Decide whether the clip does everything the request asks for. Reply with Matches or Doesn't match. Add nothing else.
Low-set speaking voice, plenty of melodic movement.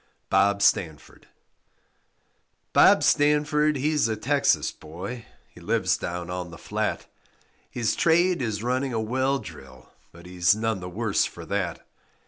Matches